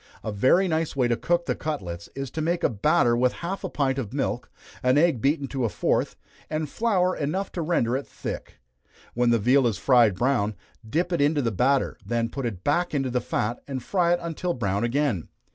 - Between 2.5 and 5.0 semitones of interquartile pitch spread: No, wide, 5.4 semitones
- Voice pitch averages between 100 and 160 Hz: Yes, low, 135 Hz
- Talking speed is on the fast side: Yes, fast, 215 wpm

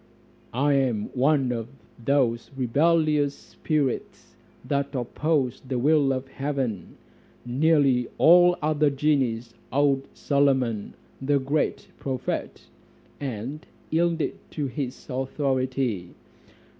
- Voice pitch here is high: No, low, 135 Hz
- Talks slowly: Yes, slow, 100 wpm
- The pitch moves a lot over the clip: No, average, 2.9 semitones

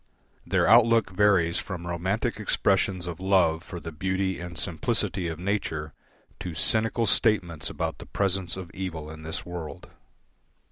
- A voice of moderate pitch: No, very low, 90 Hz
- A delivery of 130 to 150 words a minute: Yes, average, 145 wpm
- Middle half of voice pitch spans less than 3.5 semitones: Yes, average, 3.0 semitones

